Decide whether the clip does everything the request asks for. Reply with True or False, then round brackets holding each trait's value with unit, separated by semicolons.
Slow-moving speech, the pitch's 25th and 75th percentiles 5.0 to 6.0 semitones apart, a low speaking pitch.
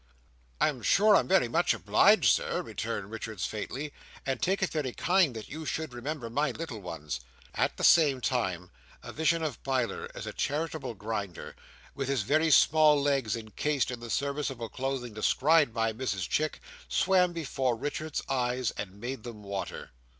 False (170 wpm; 5.3 semitones; 130 Hz)